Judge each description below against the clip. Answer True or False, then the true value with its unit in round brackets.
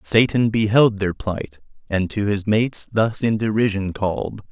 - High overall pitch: False (105 Hz)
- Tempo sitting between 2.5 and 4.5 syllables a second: True (4.3 syllables/s)